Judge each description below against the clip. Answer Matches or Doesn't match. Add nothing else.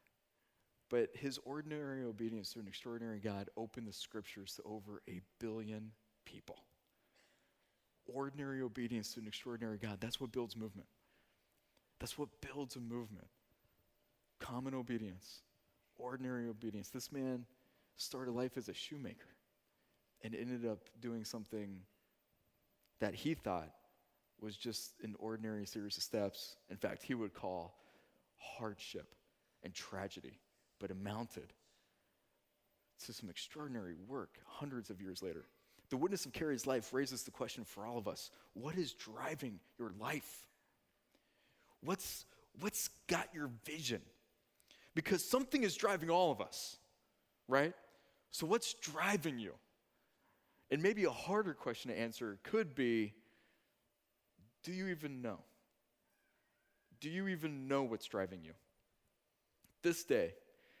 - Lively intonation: Doesn't match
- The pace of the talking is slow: Matches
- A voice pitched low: Matches